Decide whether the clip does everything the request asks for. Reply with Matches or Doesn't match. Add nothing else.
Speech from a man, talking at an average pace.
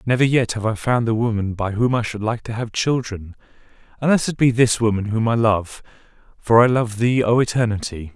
Doesn't match